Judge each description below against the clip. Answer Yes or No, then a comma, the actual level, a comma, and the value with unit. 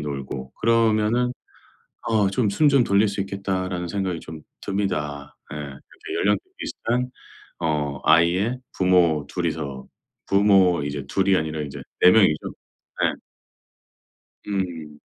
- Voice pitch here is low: Yes, very low, 90 Hz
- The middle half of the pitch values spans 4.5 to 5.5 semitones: Yes, average, 5.1 semitones